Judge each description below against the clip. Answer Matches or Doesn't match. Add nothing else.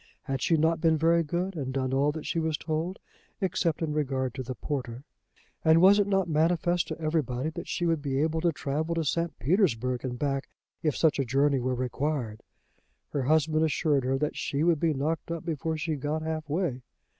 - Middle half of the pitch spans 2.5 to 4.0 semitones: Matches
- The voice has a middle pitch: Matches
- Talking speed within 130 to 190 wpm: Doesn't match